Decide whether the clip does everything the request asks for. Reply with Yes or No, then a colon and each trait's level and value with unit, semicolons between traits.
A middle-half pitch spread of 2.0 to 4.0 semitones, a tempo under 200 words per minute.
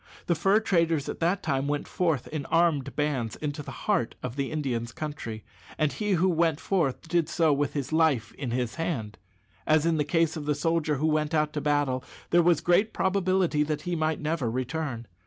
No: average, 3.1 semitones; fast, 205 wpm